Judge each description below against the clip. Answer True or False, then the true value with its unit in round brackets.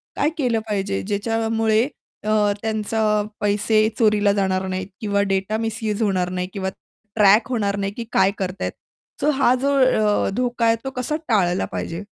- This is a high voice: True (210 Hz)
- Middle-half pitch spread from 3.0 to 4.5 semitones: False (2.4 semitones)